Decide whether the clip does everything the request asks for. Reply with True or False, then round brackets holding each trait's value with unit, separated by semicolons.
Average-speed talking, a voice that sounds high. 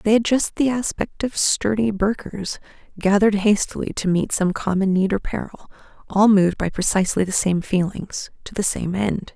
True (180 wpm; 200 Hz)